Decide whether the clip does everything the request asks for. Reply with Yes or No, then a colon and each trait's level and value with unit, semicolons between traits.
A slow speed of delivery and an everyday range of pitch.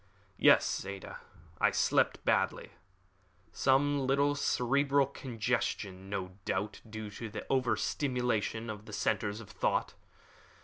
Yes: slow, 115 wpm; average, 4.5 semitones